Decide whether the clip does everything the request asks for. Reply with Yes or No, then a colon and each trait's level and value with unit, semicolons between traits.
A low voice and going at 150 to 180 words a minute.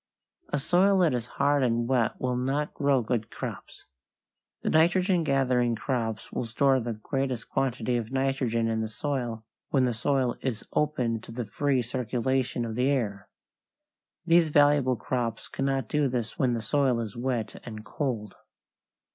Yes: low, 125 Hz; average, 160 wpm